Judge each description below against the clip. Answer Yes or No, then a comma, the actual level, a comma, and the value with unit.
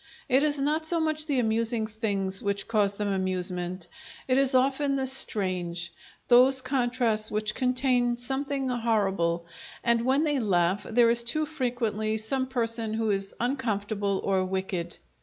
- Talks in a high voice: Yes, high, 230 Hz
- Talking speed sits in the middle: Yes, average, 150 wpm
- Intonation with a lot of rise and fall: No, average, 4.6 semitones